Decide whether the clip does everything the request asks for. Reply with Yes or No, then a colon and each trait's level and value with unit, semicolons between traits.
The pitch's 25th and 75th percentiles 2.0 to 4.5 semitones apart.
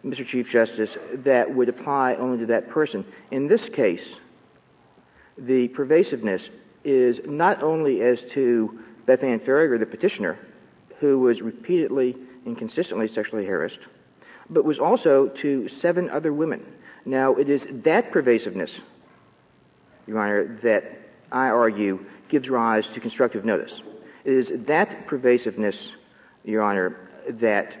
Yes: average, 3.8 semitones